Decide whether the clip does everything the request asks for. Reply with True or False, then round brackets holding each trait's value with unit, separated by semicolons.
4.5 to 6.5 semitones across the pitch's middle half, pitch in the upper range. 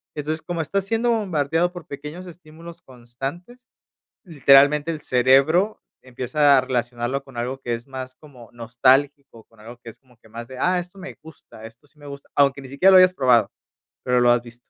False (5.1 semitones; 140 Hz)